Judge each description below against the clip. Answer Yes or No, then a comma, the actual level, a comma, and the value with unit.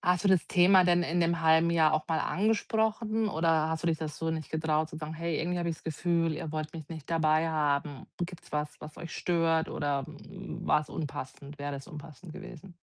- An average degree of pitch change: No, narrow, 2.0 semitones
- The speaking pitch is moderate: Yes, medium, 160 Hz